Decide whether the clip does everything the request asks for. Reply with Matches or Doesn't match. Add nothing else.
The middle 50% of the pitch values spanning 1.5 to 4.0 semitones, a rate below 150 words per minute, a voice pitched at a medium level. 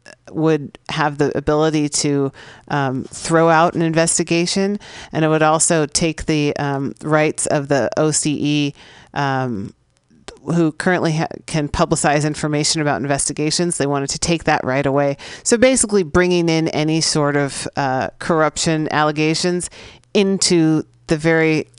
Matches